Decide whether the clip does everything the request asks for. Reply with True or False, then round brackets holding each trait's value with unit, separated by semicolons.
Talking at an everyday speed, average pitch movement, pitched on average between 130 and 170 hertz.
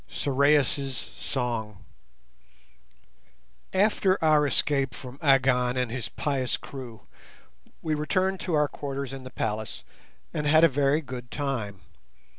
False (120 wpm; 3.0 semitones; 135 Hz)